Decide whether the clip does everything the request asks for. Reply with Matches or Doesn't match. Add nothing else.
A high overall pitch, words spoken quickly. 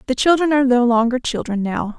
Matches